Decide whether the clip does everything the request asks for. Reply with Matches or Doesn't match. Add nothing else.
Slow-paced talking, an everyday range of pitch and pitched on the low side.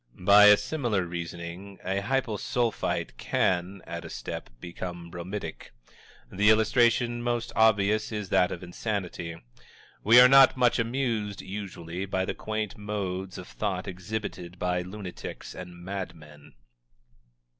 Matches